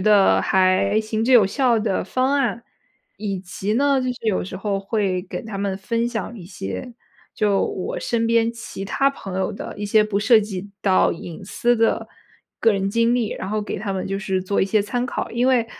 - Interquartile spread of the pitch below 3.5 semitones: Yes, average, 3.1 semitones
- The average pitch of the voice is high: Yes, high, 210 Hz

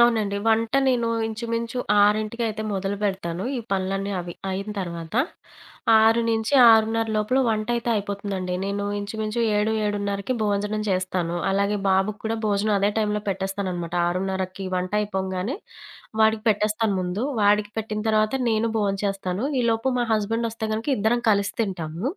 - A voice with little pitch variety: Yes, narrow, 2.3 semitones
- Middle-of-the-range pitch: No, high, 210 Hz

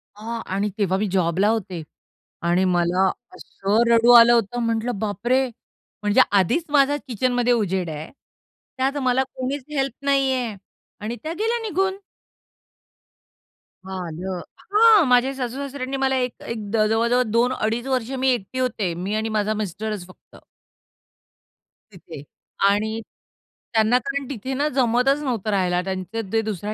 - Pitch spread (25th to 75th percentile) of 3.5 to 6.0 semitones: Yes, average, 4.6 semitones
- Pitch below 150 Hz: No, high, 230 Hz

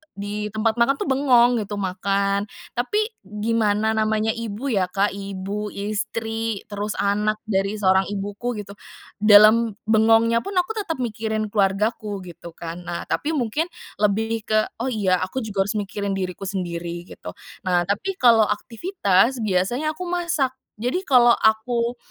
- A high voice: Yes, high, 215 Hz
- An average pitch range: Yes, average, 3.0 semitones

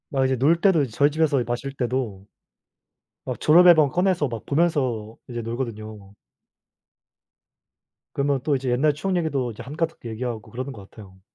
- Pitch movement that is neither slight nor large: Yes, average, 4.7 semitones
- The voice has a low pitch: Yes, low, 130 Hz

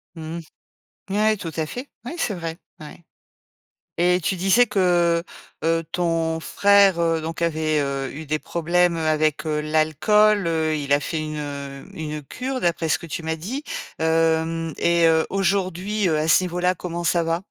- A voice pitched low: No, medium, 165 Hz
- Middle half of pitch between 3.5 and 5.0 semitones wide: No, narrow, 2.4 semitones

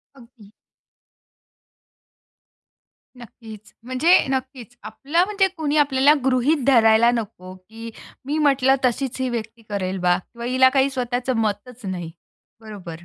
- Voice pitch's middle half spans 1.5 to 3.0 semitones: No, average, 3.6 semitones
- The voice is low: No, high, 245 Hz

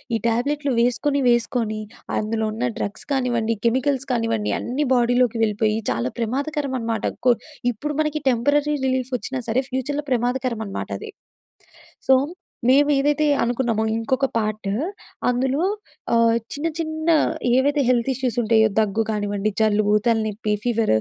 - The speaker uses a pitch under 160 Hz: No, high, 245 Hz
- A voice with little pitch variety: No, average, 3.5 semitones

